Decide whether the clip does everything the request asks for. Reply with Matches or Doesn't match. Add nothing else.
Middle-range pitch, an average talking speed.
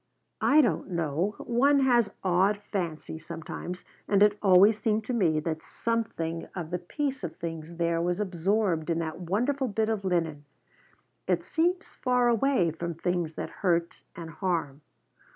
Matches